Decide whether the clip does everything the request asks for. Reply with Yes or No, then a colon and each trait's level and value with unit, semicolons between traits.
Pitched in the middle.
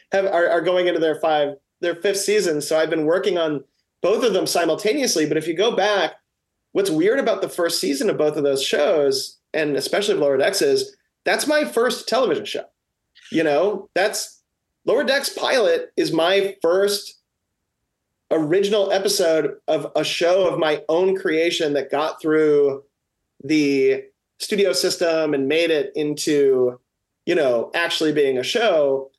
Yes: medium, 170 Hz